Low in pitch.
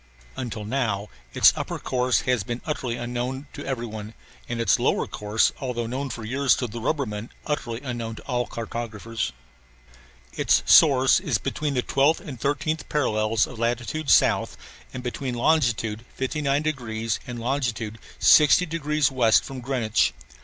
Yes: low, 125 Hz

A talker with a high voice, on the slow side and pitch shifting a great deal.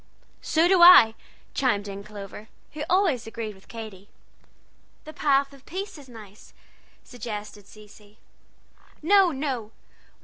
Yes: high, 230 Hz; slow, 125 wpm; wide, 6.5 semitones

